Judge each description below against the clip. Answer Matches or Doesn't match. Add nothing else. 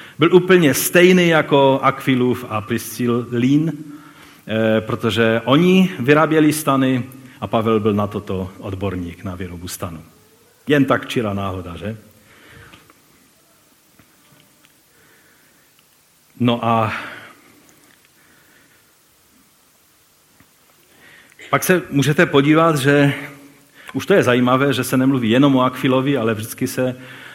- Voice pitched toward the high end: Doesn't match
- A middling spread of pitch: Matches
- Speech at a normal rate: Doesn't match